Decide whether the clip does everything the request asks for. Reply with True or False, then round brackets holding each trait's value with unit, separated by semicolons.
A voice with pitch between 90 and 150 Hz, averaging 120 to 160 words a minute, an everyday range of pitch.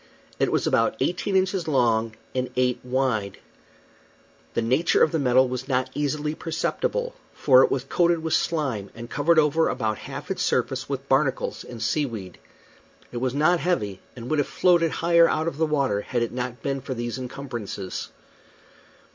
False (135 Hz; 175 wpm; 4.7 semitones)